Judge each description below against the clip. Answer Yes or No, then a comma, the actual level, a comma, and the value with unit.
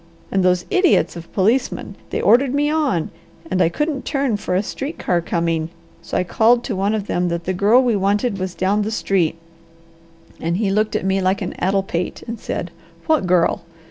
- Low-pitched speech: No, high, 195 Hz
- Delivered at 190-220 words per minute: Yes, fast, 205 wpm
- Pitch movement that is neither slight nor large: Yes, average, 4.7 semitones